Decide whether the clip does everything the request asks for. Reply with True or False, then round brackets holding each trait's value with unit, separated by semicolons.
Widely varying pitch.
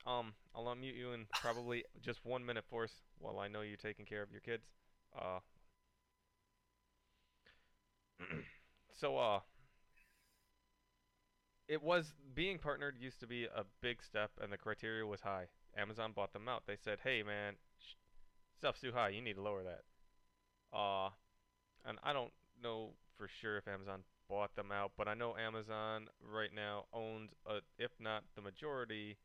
False (3.0 semitones)